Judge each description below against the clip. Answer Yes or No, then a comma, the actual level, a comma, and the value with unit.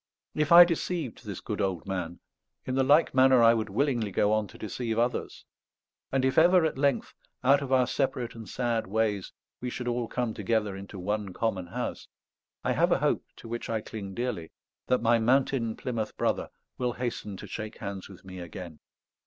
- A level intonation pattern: No, average, 4.2 semitones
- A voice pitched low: Yes, low, 115 Hz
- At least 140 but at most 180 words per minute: No, average, 195 wpm